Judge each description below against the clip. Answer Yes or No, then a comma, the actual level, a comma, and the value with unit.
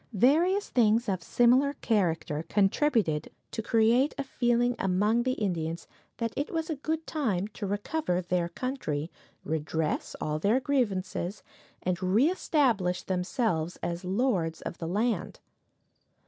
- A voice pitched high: Yes, high, 210 Hz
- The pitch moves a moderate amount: No, wide, 6.3 semitones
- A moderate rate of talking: No, slow, 130 wpm